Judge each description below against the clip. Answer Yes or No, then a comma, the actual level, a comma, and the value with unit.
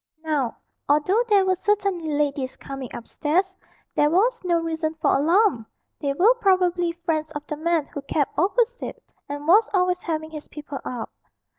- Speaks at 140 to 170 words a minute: Yes, average, 160 wpm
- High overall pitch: Yes, very high, 325 Hz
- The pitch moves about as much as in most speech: Yes, average, 4.2 semitones